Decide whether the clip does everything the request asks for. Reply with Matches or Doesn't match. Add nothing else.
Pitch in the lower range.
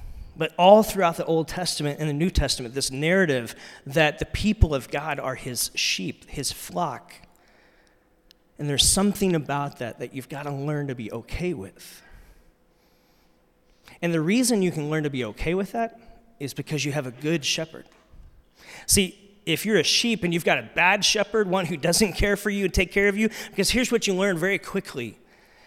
Doesn't match